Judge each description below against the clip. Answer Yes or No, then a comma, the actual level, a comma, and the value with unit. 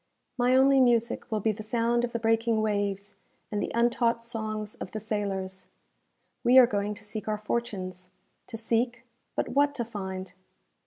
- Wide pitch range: No, narrow, 2.5 semitones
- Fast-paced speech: No, average, 170 wpm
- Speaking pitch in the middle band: No, high, 220 Hz